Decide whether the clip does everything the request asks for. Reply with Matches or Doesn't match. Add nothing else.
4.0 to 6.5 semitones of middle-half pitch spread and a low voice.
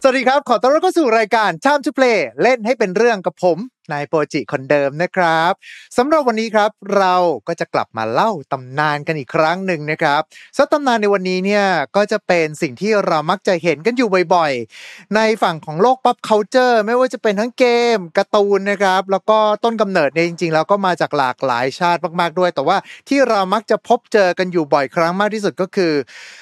Doesn't match